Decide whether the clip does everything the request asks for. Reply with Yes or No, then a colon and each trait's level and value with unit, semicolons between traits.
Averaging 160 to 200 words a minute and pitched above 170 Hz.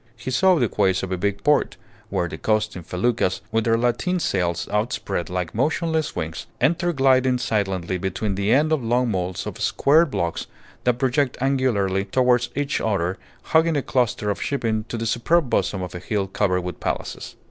No: average, 180 wpm; low, 115 Hz